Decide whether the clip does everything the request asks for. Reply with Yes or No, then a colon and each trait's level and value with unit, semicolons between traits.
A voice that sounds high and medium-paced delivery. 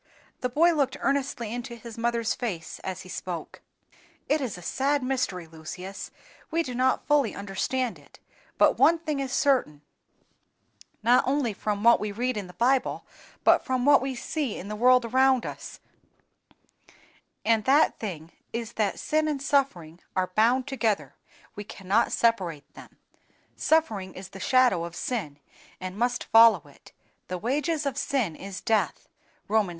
Yes: high, 235 Hz; average, 160 wpm